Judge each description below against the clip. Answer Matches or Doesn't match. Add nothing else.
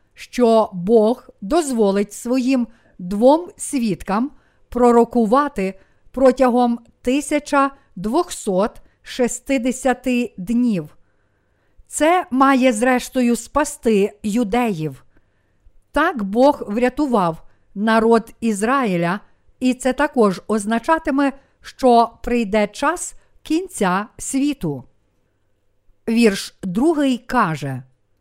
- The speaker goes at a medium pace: Doesn't match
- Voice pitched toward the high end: Matches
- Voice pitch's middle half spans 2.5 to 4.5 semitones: Doesn't match